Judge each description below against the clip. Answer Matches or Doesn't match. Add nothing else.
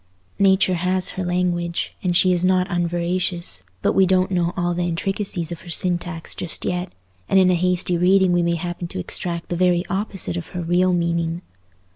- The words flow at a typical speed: Matches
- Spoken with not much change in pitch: Matches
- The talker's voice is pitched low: Doesn't match